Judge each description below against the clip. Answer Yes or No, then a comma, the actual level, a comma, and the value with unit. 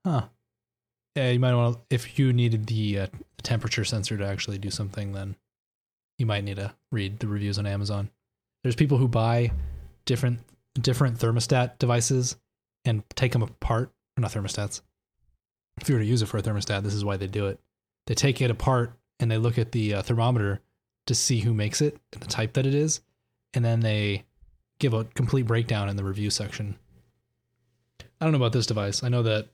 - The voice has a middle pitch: No, low, 115 Hz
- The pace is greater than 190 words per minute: Yes, average, 200 wpm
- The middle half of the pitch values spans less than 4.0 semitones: Yes, average, 3.1 semitones